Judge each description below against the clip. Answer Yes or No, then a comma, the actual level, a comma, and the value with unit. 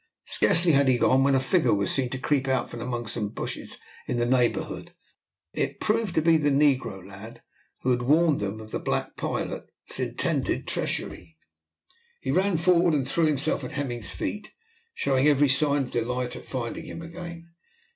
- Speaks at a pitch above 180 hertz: No, low, 135 Hz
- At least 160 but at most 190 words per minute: Yes, average, 180 wpm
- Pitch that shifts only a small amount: No, average, 4.8 semitones